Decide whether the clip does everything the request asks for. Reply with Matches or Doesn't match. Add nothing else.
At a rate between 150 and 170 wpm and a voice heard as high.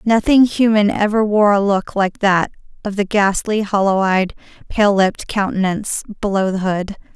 Matches